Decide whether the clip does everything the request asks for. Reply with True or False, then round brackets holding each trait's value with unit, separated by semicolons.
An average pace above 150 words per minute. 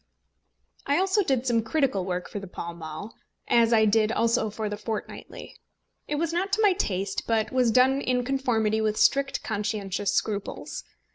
True (170 wpm)